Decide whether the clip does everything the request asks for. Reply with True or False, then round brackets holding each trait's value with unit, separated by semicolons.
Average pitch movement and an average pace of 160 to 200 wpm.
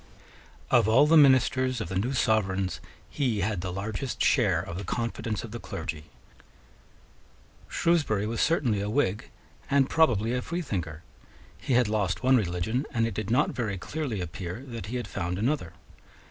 True (5.0 semitones; 165 wpm)